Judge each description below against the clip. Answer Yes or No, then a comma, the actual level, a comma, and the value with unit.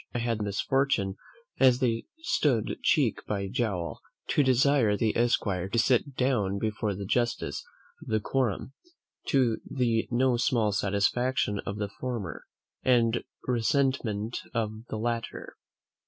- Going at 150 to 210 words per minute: No, slow, 135 wpm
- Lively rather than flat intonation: No, average, 3.6 semitones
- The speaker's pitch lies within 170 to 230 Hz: No, low, 115 Hz